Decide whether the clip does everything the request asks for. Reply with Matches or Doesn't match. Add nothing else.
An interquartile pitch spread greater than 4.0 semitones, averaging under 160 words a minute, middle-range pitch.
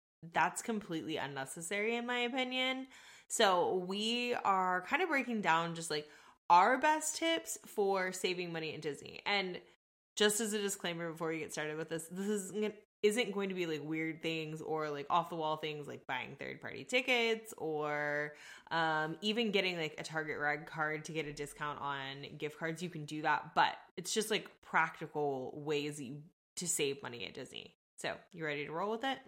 Doesn't match